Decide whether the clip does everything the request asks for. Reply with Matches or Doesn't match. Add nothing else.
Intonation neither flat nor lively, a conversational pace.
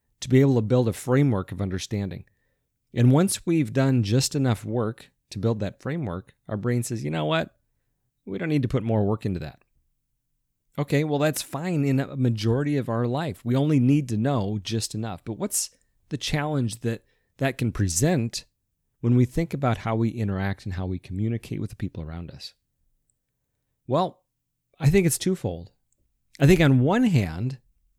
Matches